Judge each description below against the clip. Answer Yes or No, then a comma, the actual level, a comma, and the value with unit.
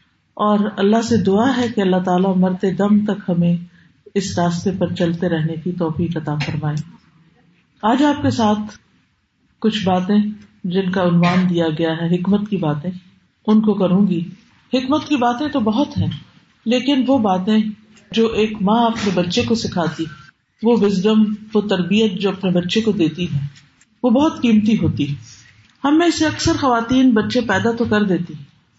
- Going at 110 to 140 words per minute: No, average, 170 wpm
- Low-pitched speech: No, high, 200 Hz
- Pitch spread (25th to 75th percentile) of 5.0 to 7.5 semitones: No, average, 4.1 semitones